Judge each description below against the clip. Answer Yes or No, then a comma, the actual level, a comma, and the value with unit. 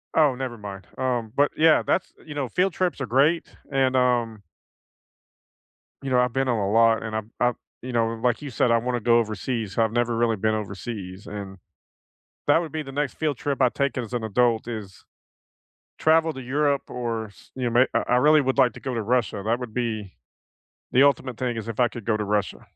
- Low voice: Yes, low, 120 Hz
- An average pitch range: Yes, average, 3.2 semitones